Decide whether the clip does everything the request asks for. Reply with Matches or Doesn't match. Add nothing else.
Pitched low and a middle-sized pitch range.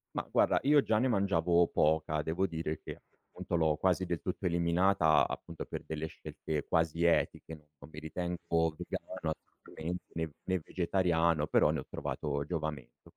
Doesn't match